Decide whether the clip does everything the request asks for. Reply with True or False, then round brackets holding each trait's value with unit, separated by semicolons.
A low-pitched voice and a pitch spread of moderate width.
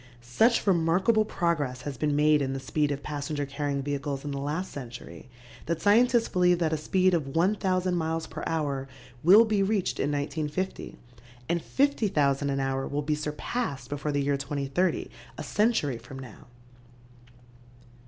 False (150 Hz; 4.7 semitones)